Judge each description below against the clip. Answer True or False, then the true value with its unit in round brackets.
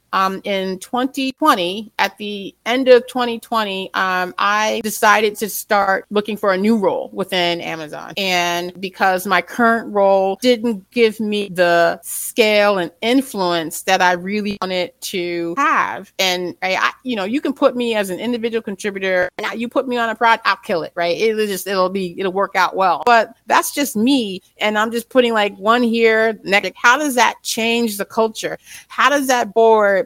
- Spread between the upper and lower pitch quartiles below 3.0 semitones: False (3.7 semitones)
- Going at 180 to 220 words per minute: True (185 wpm)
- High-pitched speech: True (210 Hz)